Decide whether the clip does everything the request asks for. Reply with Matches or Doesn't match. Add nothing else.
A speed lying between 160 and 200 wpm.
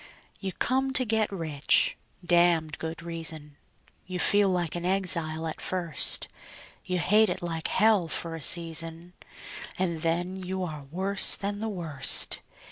Doesn't match